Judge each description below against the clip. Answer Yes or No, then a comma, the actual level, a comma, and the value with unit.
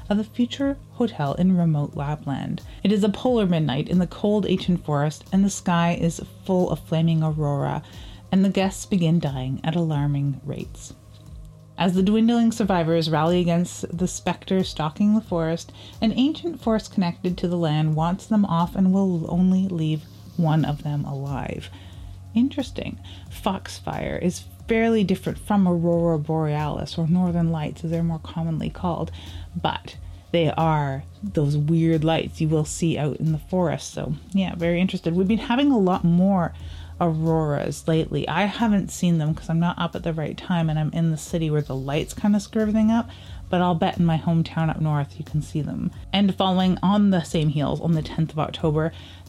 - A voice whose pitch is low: No, medium, 165 Hz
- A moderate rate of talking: Yes, average, 185 wpm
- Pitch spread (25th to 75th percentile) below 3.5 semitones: No, average, 3.9 semitones